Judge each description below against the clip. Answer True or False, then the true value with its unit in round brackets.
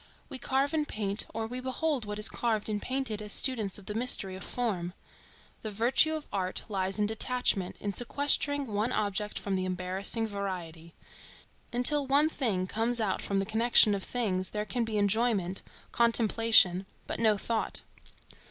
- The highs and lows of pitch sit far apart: False (3.8 semitones)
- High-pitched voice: True (215 Hz)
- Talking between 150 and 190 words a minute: True (170 wpm)